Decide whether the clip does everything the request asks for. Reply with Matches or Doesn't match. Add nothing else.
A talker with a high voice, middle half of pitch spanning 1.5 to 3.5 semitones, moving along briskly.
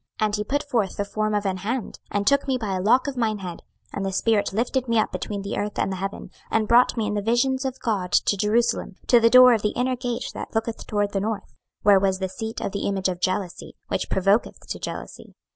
Matches